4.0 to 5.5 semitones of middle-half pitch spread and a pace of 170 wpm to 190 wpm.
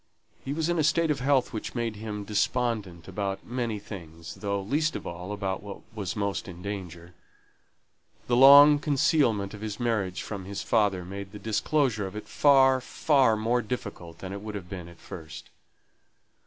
Yes: average, 4.6 semitones; average, 180 wpm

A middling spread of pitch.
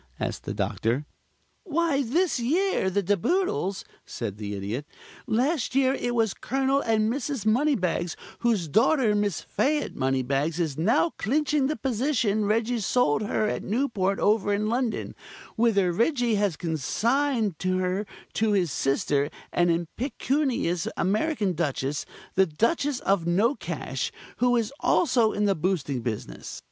No: wide, 7.1 semitones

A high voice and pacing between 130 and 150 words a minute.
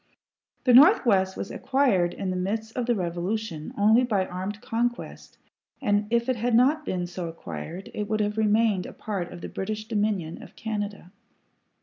No: high, 210 Hz; average, 175 wpm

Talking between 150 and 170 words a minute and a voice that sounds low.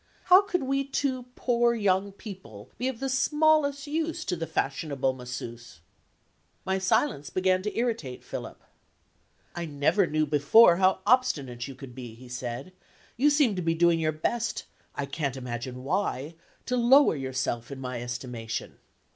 No: average, 155 wpm; medium, 170 Hz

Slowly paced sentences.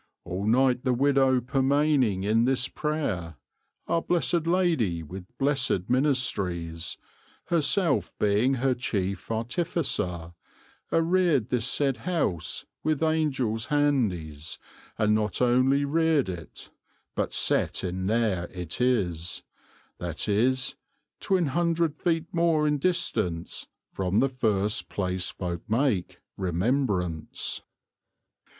Yes: slow, 110 wpm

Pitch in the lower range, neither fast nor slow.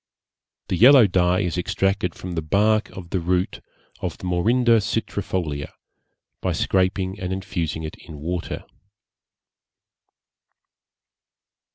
No: very low, 95 Hz; slow, 110 wpm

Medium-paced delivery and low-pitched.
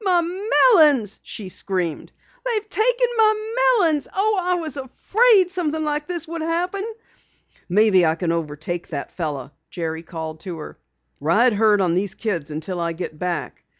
No: average, 155 wpm; high, 235 Hz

